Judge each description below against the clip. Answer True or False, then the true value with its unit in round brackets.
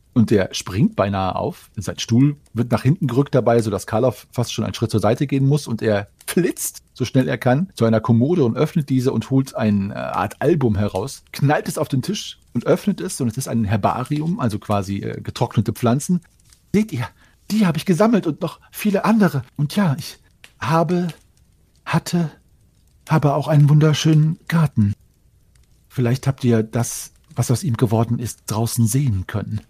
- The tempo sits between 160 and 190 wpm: True (185 wpm)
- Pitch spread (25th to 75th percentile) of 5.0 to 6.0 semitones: True (5.3 semitones)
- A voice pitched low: True (125 Hz)